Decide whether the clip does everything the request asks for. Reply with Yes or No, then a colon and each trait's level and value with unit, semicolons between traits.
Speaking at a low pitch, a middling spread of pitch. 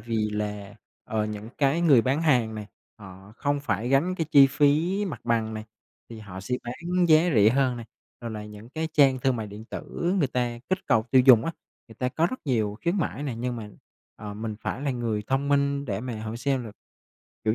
Yes: low, 120 Hz; average, 4.7 semitones